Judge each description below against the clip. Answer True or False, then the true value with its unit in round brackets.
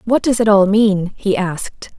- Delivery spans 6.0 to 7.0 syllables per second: False (4.4 syllables/s)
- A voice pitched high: True (205 Hz)